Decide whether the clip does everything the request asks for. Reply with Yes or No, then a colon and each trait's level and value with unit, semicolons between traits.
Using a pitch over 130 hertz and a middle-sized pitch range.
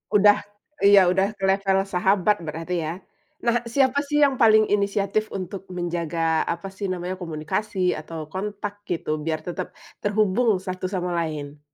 Yes: high, 190 Hz; average, 3.3 semitones